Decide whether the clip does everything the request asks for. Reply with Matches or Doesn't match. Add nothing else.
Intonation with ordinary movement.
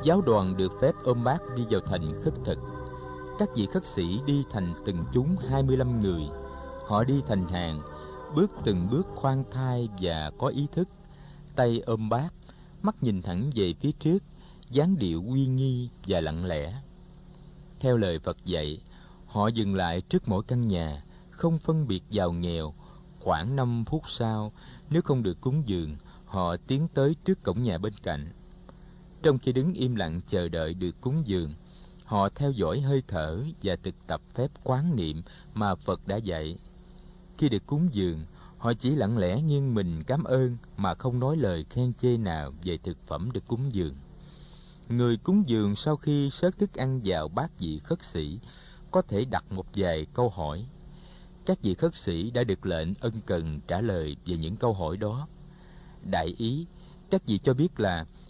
Doesn't match